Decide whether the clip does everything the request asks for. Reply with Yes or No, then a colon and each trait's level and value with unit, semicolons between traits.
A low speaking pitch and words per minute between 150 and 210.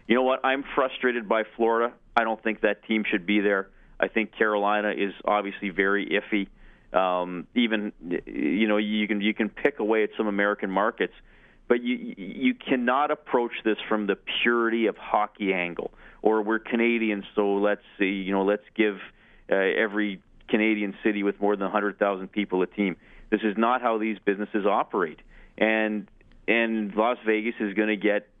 Yes: low, 105 Hz; average, 180 wpm